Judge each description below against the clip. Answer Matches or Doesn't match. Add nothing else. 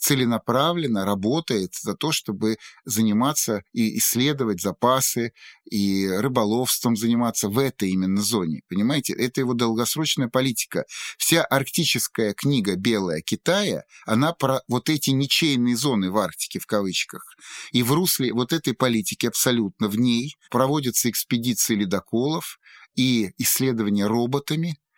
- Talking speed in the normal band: Matches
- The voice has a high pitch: Doesn't match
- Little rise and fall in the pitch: Doesn't match